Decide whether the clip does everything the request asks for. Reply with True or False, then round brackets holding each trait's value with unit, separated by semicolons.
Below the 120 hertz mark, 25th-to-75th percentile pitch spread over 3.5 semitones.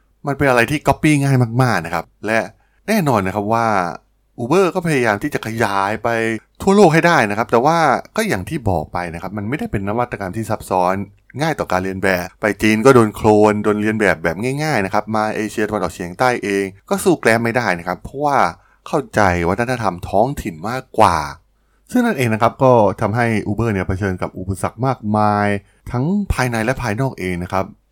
True (110 Hz; 4.4 semitones)